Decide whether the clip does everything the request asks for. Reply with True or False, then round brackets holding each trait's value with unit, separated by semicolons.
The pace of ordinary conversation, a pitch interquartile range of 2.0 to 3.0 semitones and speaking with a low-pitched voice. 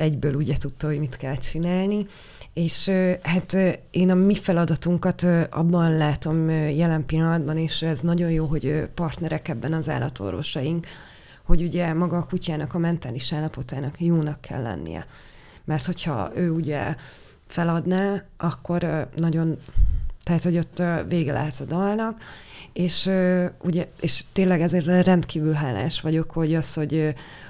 False (135 wpm; 2.5 semitones; 160 Hz)